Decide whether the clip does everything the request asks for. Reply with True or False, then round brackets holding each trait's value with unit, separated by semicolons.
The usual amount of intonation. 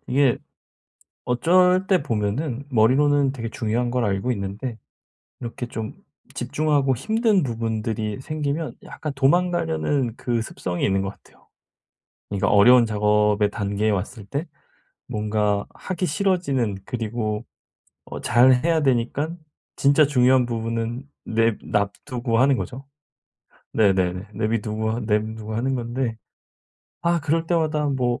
True (4.8 semitones)